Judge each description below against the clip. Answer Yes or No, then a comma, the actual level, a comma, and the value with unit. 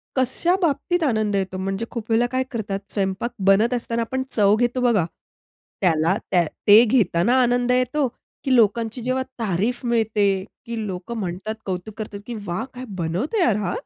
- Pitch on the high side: Yes, high, 225 Hz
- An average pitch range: Yes, average, 4.1 semitones